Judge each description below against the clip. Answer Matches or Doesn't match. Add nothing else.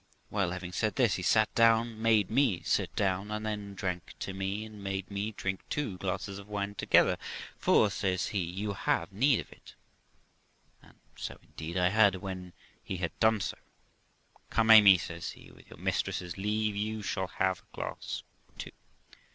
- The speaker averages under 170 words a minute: Doesn't match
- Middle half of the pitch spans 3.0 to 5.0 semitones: Doesn't match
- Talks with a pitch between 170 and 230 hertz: Doesn't match